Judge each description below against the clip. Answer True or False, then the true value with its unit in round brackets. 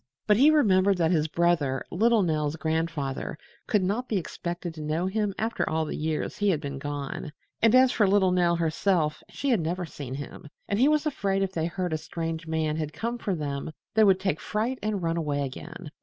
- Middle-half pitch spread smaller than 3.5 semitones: False (4.6 semitones)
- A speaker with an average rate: False (215 wpm)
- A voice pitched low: False (170 Hz)